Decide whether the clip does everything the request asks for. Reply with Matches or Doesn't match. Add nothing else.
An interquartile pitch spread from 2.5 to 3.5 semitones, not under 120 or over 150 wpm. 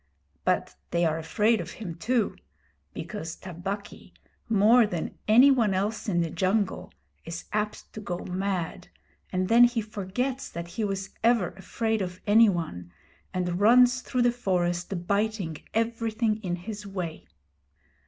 Doesn't match